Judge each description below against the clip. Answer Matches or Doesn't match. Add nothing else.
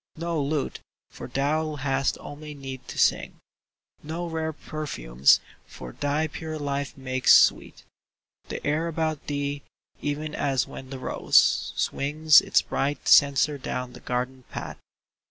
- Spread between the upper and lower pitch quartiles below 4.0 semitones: Matches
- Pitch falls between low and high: Matches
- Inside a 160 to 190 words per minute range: Doesn't match